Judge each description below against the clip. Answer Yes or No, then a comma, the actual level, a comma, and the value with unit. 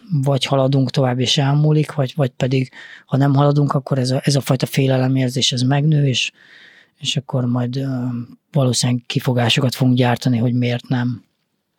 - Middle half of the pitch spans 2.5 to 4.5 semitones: No, narrow, 2.0 semitones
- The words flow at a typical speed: No, fast, 160 wpm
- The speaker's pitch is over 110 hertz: Yes, low, 135 Hz